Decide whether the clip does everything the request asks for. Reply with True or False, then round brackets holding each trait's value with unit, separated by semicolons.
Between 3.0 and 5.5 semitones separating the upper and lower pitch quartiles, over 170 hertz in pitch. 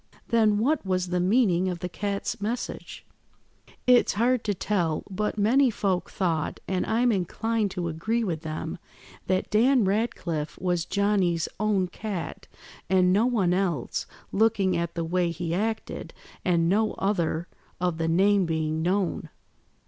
True (3.8 semitones; 190 Hz)